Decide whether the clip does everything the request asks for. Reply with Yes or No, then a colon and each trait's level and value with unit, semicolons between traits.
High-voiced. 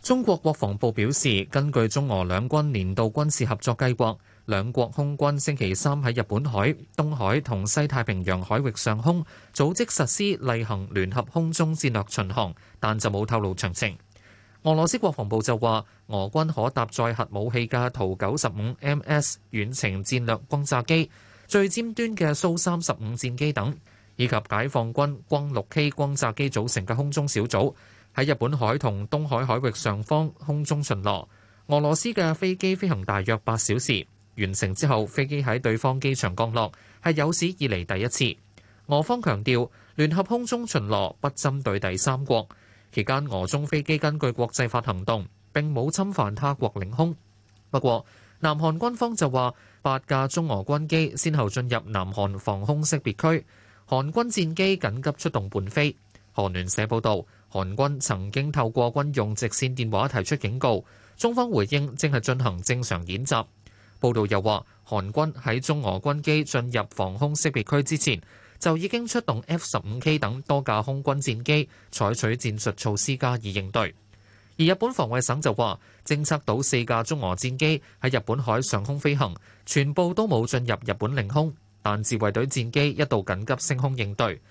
No: low, 125 Hz